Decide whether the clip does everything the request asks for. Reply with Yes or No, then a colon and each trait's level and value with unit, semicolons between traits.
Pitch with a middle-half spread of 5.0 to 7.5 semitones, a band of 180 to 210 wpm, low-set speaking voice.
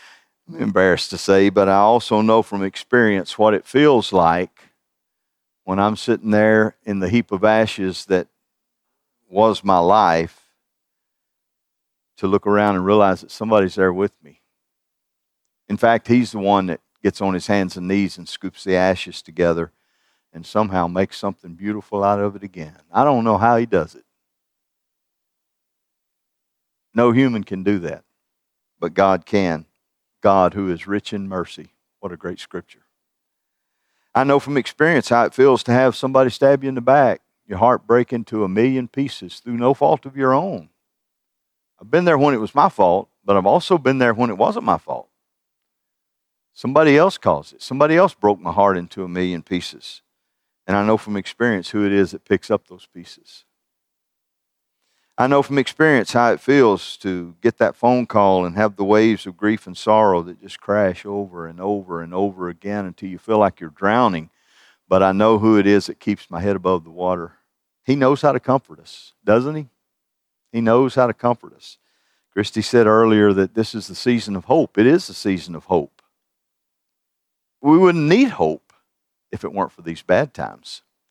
No: average, 4.1 semitones; average, 185 wpm; low, 100 Hz